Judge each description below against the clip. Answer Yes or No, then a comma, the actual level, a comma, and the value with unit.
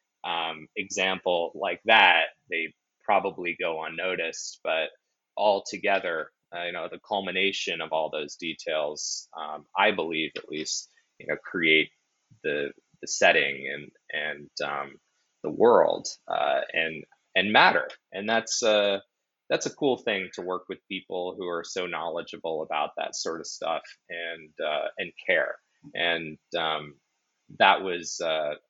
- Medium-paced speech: Yes, average, 145 wpm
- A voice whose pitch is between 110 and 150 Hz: No, very low, 85 Hz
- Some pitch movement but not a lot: Yes, average, 3.0 semitones